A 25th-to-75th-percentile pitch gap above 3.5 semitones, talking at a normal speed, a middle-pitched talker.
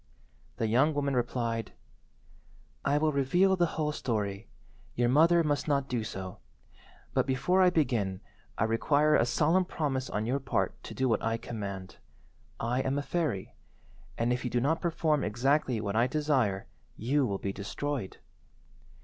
No: average, 4.8 semitones; average, 160 wpm; low, 130 Hz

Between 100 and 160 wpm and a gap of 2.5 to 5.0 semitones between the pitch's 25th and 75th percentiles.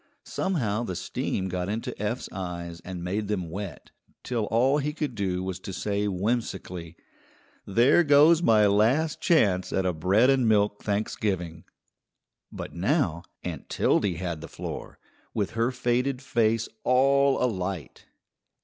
No: average, 140 wpm; wide, 5.5 semitones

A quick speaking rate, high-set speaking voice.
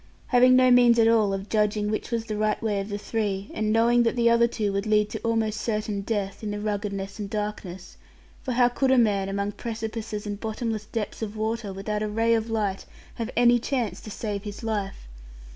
Yes: fast, 215 wpm; high, 215 Hz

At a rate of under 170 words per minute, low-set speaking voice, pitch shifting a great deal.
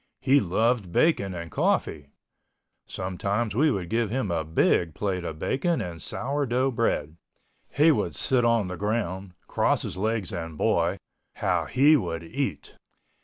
Yes: average, 155 wpm; low, 100 Hz; wide, 6.4 semitones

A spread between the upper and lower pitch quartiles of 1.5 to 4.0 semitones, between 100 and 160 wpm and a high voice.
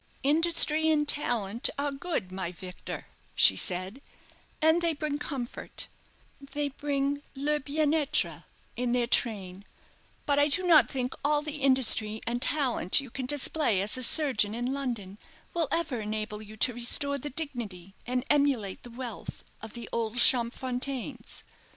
No: average, 4.8 semitones; average, 150 wpm; very high, 260 Hz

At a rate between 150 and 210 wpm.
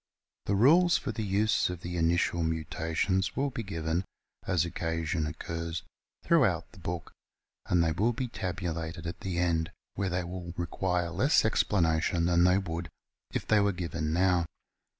Yes: average, 160 wpm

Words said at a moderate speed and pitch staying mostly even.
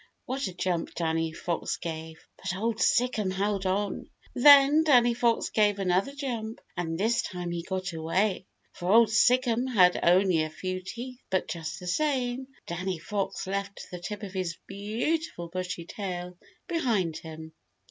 No: average, 160 wpm; average, 4.8 semitones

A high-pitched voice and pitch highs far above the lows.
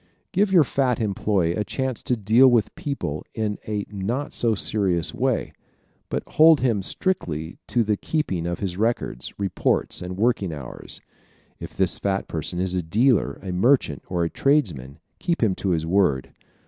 No: low, 100 Hz; wide, 5.9 semitones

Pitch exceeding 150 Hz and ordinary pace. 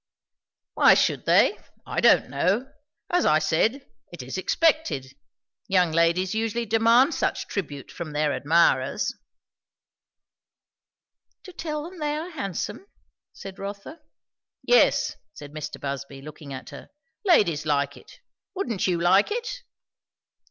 No: high, 190 Hz; slow, 125 wpm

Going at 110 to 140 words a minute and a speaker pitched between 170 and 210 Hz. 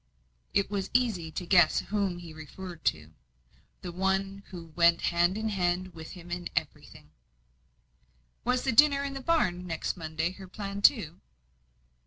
No: average, 155 wpm; medium, 185 Hz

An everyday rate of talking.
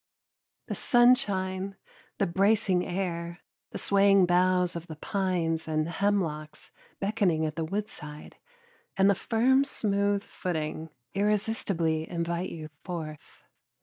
No: slow, 115 wpm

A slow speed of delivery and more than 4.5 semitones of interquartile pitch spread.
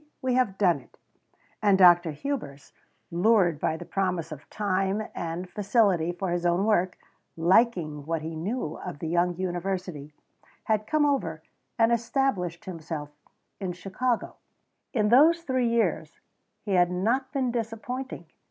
No: average, 145 wpm; average, 5.1 semitones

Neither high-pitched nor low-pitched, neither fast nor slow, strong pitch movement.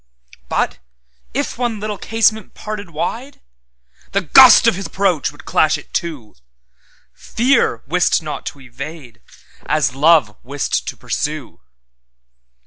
No: medium, 155 Hz; slow, 115 wpm; wide, 8.9 semitones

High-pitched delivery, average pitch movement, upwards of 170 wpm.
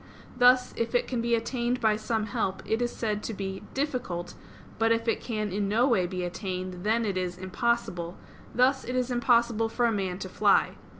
Yes: high, 225 Hz; average, 3.9 semitones; average, 200 wpm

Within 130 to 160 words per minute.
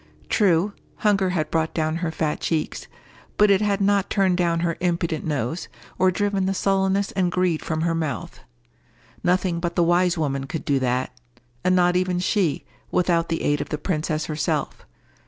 No: average, 175 wpm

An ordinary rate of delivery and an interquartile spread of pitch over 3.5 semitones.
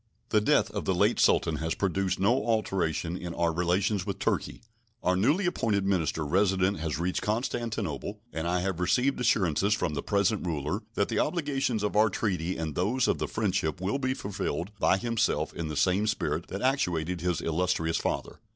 Yes: average, 180 wpm; average, 4.1 semitones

